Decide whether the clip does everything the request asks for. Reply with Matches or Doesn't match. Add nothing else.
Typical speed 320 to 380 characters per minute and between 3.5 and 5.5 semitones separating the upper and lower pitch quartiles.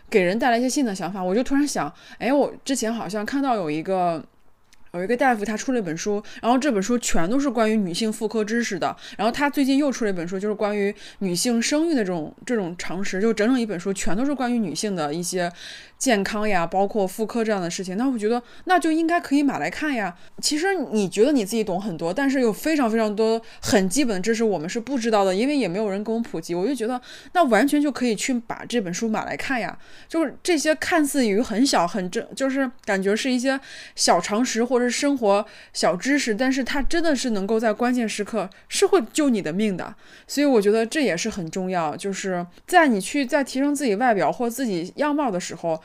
Matches